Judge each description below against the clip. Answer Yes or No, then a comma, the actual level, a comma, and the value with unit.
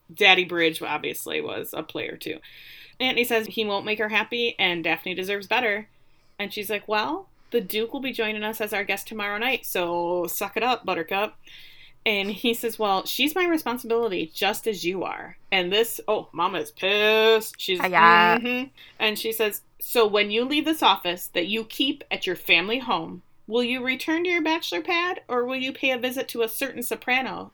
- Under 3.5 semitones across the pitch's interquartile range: No, average, 4.0 semitones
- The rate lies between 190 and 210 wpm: Yes, average, 200 wpm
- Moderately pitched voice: No, high, 220 Hz